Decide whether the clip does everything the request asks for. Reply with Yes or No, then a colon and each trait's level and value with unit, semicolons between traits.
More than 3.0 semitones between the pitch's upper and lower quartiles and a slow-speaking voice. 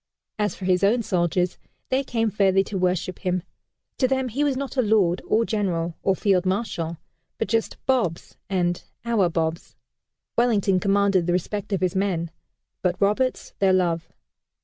No: average, 3.6 semitones; average, 165 wpm